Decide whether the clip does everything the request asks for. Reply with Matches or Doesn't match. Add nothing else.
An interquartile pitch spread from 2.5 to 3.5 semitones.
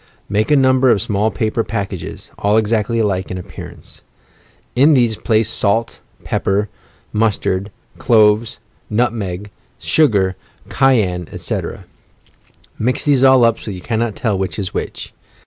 Matches